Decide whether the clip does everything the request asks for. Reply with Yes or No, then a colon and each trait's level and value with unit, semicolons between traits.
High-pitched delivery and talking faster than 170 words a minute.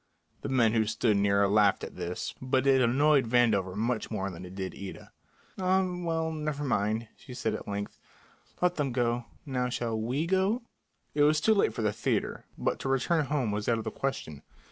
No: low, 120 Hz; average, 200 wpm